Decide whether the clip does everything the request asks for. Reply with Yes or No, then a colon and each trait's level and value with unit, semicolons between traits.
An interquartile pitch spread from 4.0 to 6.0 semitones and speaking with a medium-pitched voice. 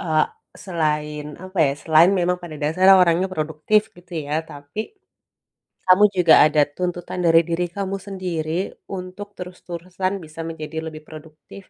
No: average, 2.9 semitones; medium, 170 Hz